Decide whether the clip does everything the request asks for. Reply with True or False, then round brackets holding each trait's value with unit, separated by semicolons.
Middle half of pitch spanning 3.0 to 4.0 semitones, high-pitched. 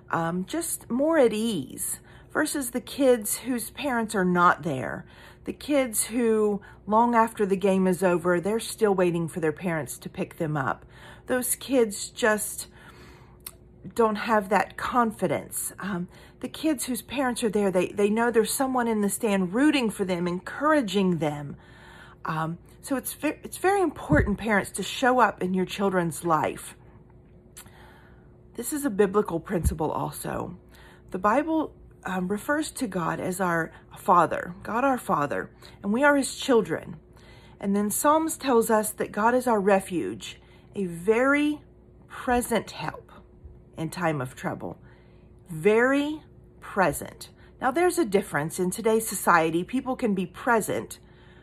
False (5.5 semitones; 210 Hz)